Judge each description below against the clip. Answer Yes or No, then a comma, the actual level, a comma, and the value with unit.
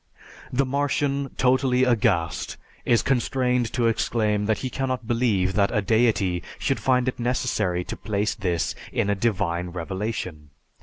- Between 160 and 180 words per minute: No, average, 145 wpm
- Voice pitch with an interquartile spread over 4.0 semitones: Yes, average, 4.7 semitones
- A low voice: Yes, low, 115 Hz